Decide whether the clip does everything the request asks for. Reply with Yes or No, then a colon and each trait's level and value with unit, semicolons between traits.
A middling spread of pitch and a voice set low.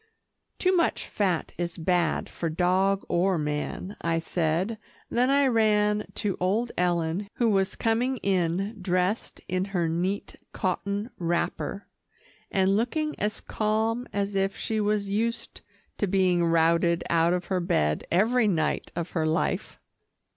No: average, 3.7 semitones; high, 190 Hz